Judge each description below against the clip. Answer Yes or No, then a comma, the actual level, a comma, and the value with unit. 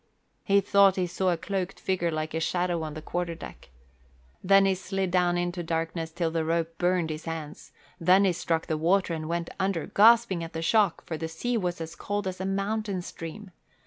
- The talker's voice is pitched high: No, medium, 175 Hz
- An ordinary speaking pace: No, fast, 210 wpm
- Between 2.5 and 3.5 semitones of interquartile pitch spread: Yes, average, 2.8 semitones